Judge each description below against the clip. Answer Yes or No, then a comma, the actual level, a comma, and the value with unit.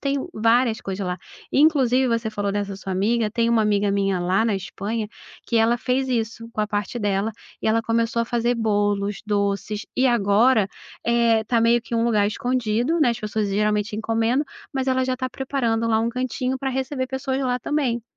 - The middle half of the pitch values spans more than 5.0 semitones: No, average, 3.2 semitones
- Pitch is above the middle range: Yes, high, 230 Hz